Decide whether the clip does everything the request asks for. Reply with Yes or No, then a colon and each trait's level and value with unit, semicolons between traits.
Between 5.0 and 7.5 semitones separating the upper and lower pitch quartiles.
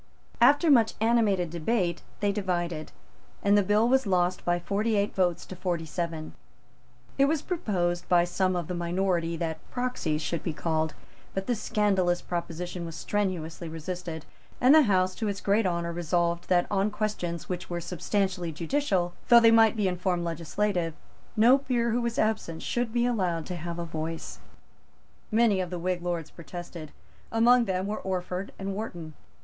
No: average, 3.8 semitones